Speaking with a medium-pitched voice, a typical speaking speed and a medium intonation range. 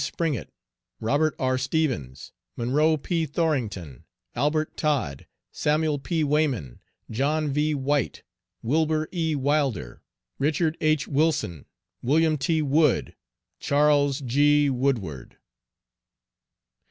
No: medium, 145 Hz; slow, 95 wpm; average, 3.2 semitones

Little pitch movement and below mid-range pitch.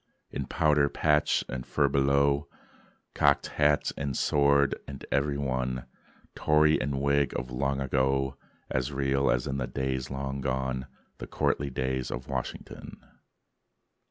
Yes: narrow, 1.4 semitones; very low, 70 Hz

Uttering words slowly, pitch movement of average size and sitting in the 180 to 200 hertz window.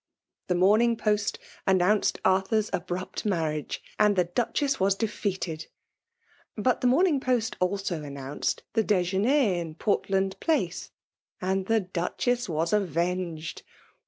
Yes: slow, 130 wpm; average, 3.8 semitones; high, 190 Hz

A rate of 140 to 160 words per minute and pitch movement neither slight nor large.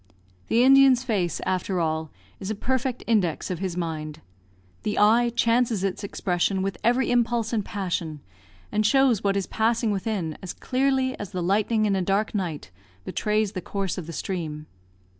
No: average, 170 wpm; average, 4.4 semitones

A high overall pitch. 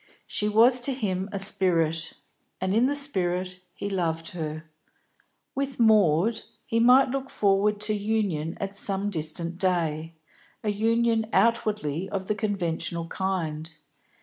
Yes: high, 195 Hz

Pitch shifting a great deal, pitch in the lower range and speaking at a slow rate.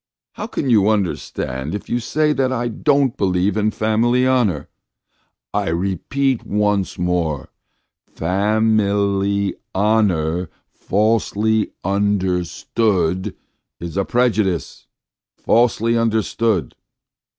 No: average, 3.7 semitones; low, 105 Hz; slow, 115 wpm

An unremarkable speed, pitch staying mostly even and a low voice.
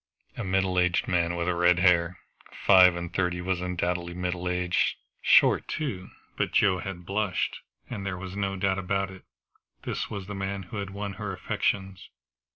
Yes: average, 170 wpm; narrow, 1.6 semitones; very low, 95 Hz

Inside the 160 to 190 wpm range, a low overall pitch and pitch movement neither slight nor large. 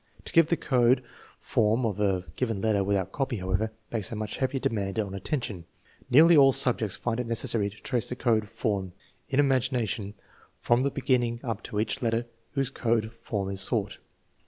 Yes: average, 180 wpm; low, 115 Hz; average, 3.8 semitones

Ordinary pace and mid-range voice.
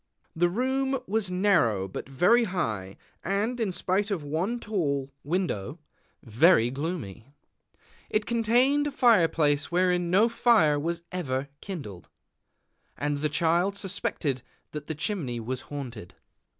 No: slow, 130 wpm; medium, 170 Hz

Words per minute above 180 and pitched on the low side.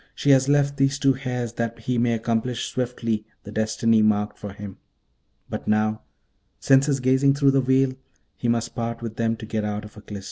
Yes: average, 200 wpm; low, 115 Hz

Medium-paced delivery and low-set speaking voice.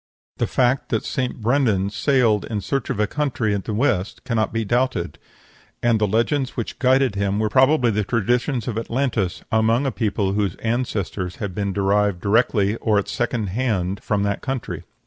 Yes: average, 180 wpm; low, 110 Hz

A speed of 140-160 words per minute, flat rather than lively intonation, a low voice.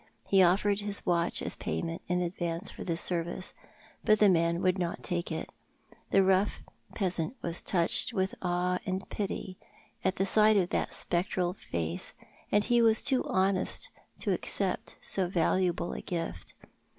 No: average, 150 wpm; narrow, 2.3 semitones; medium, 185 Hz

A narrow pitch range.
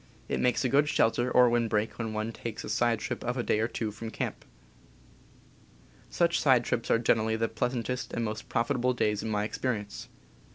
Yes: narrow, 2.1 semitones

